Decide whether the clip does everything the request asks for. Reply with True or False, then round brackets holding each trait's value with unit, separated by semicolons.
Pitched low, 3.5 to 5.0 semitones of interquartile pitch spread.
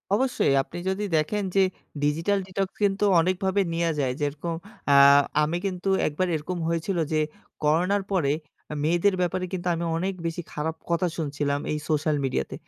False (170 Hz; 3.8 semitones)